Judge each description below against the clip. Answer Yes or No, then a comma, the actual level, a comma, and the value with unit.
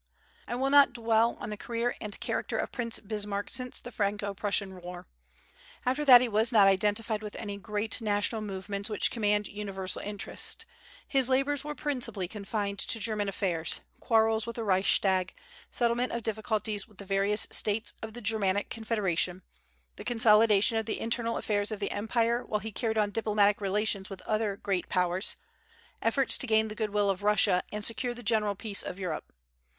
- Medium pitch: No, high, 210 Hz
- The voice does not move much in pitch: Yes, narrow, 2.3 semitones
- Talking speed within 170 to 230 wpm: Yes, average, 180 wpm